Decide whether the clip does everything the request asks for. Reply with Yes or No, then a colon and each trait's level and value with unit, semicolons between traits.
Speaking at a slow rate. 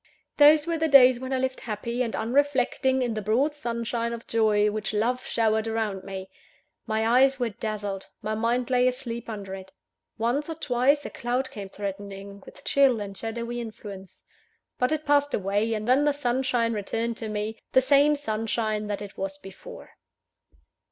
No: average, 175 wpm